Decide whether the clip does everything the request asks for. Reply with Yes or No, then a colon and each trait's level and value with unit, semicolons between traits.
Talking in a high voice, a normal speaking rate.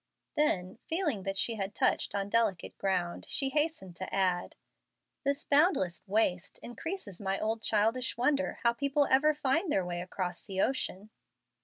Yes: high, 220 Hz; average, 155 wpm